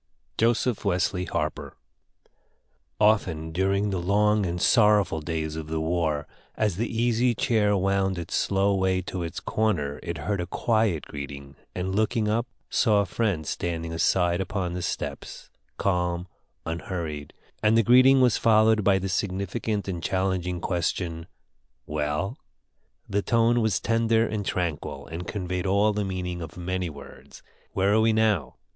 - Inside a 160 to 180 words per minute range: No, average, 150 wpm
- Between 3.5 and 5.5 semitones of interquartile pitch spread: Yes, average, 4.0 semitones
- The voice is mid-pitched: No, very low, 95 Hz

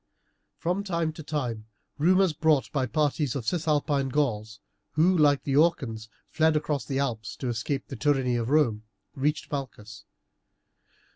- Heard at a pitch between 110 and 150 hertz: Yes, medium, 140 Hz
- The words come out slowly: No, average, 145 wpm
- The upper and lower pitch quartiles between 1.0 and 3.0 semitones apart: No, average, 4.3 semitones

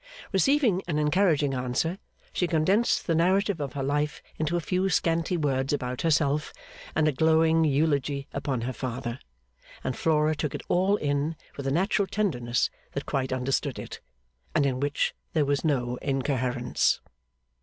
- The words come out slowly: No, average, 155 wpm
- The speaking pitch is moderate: Yes, medium, 150 Hz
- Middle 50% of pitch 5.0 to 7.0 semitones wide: No, average, 3.6 semitones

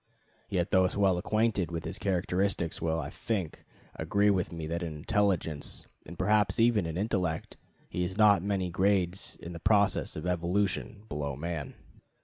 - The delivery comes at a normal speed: Yes, average, 160 wpm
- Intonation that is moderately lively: Yes, average, 3.3 semitones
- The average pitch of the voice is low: Yes, very low, 90 Hz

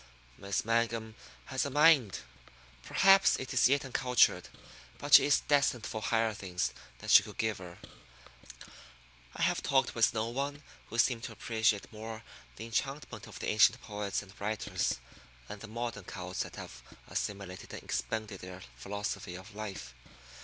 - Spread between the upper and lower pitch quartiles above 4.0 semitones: No, average, 3.6 semitones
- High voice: No, low, 110 Hz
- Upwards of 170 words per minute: No, average, 160 wpm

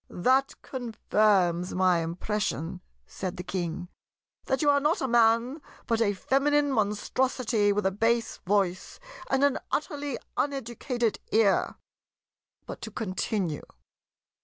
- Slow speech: Yes, slow, 120 wpm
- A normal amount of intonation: No, wide, 5.8 semitones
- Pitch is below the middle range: No, high, 220 Hz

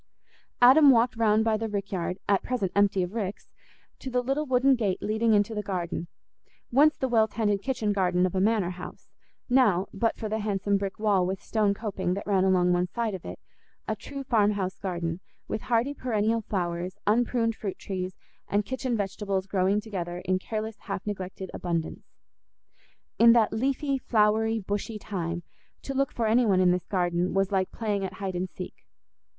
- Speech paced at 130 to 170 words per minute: No, average, 180 wpm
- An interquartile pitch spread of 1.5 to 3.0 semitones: No, average, 3.4 semitones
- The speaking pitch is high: Yes, high, 205 Hz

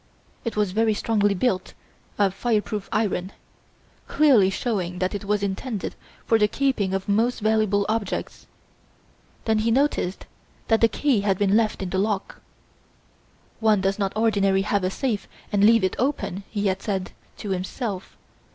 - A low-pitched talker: No, high, 205 Hz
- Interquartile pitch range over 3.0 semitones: No, narrow, 2.6 semitones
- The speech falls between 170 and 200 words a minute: No, average, 160 wpm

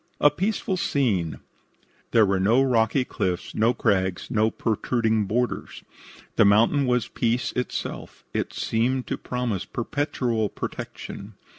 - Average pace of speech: No, slow, 125 wpm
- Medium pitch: No, low, 115 Hz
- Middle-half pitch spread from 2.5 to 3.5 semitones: Yes, average, 3.2 semitones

